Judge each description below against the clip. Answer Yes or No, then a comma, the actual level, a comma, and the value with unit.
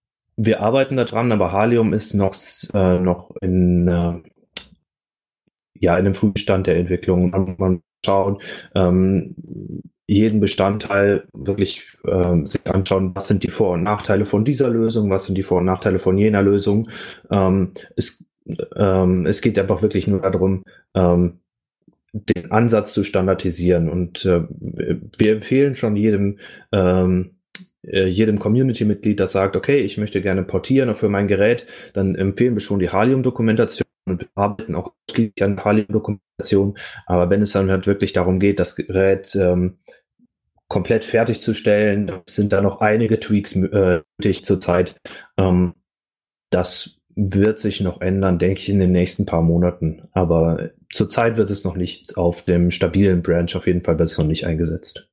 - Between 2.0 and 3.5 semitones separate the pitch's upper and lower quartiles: Yes, narrow, 2.5 semitones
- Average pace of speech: Yes, average, 155 wpm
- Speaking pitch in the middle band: No, very low, 95 Hz